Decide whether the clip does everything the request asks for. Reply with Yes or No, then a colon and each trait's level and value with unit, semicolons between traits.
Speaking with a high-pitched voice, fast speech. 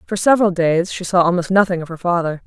No: medium, 180 Hz; fast, 245 wpm